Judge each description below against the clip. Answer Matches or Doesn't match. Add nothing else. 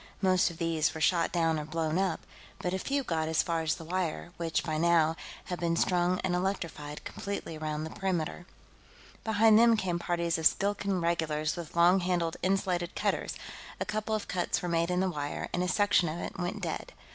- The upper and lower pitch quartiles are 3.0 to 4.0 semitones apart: Doesn't match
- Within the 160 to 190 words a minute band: Doesn't match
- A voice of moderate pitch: Matches